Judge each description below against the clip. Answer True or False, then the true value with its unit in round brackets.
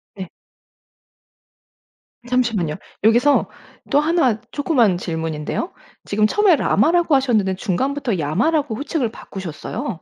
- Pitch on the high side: True (235 Hz)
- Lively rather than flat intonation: True (7.3 semitones)